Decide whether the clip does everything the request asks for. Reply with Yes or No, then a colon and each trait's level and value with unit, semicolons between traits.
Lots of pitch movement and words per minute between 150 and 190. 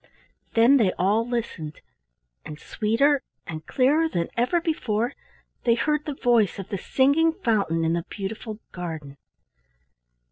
No: wide, 7.1 semitones; slow, 135 wpm